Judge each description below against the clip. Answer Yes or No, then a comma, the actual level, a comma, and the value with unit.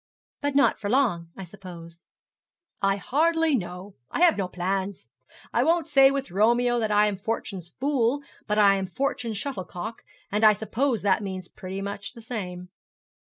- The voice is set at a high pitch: Yes, high, 210 Hz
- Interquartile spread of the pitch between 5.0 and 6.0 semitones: Yes, average, 5.3 semitones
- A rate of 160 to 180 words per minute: Yes, average, 170 wpm